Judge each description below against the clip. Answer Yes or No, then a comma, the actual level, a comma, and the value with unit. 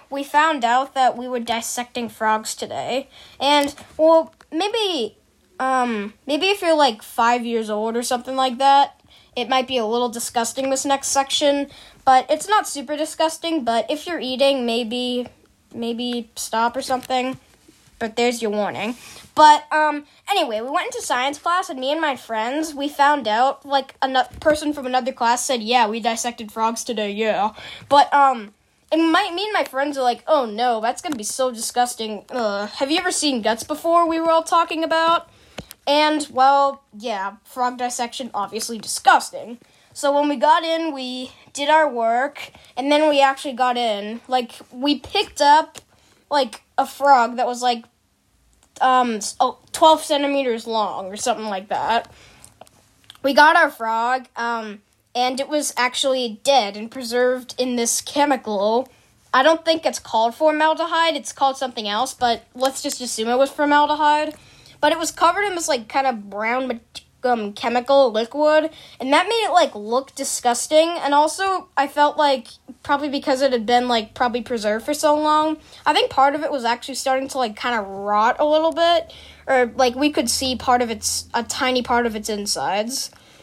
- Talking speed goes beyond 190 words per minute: No, average, 175 wpm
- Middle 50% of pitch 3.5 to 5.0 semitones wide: Yes, average, 4.0 semitones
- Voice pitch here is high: Yes, very high, 265 Hz